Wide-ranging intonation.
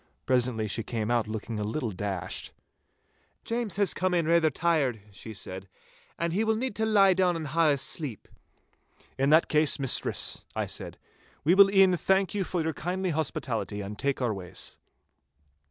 Yes: wide, 8.6 semitones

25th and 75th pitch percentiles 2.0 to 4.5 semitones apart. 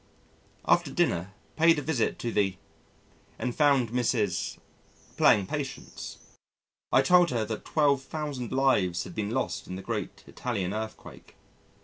No: wide, 5.5 semitones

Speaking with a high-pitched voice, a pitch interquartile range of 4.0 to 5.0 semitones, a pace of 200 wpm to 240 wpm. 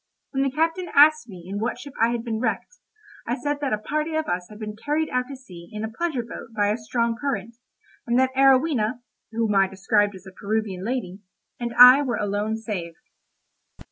Yes: high, 230 Hz; average, 4.5 semitones; fast, 205 wpm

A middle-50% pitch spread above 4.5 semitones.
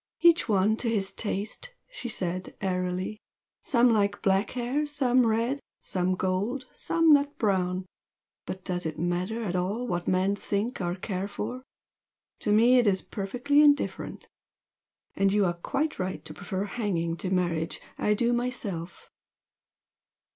Yes: average, 4.9 semitones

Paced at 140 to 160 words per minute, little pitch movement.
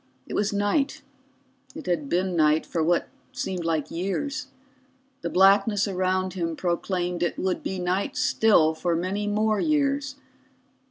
No: average, 145 wpm; average, 3.2 semitones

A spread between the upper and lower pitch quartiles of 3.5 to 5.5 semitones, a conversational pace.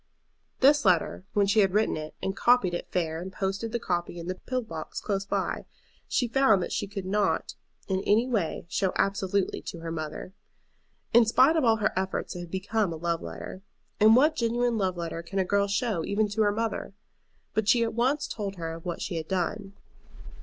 No: average, 4.1 semitones; fast, 210 wpm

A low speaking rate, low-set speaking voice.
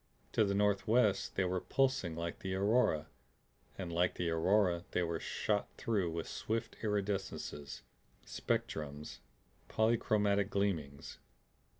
Yes: slow, 115 wpm; very low, 95 Hz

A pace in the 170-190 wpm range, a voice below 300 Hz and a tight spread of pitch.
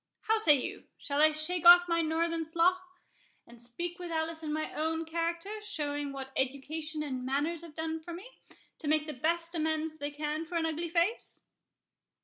No: average, 180 wpm; very high, 320 Hz; narrow, 2.0 semitones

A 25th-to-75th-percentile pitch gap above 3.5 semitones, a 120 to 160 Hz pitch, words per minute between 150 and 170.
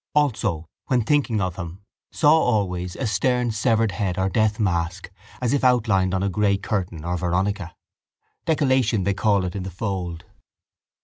No: average, 4.1 semitones; low, 100 Hz; average, 165 wpm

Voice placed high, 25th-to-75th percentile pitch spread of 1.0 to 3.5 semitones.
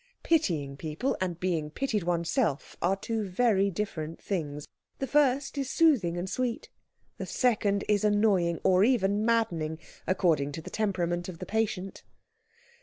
No: high, 195 Hz; average, 4.8 semitones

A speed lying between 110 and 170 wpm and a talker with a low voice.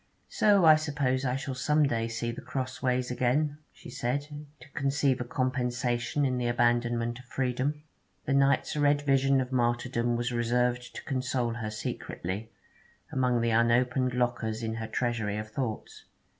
Yes: average, 155 wpm; low, 125 Hz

